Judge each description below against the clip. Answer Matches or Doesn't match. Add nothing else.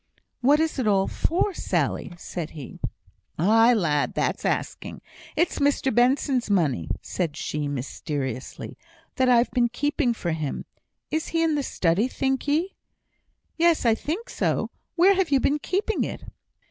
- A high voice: Matches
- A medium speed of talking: Matches